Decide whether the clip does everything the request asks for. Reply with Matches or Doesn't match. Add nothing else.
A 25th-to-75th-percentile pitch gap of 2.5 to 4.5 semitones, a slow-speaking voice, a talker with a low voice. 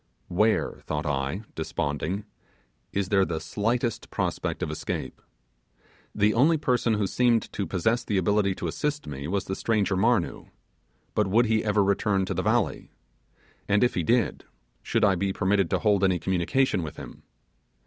Doesn't match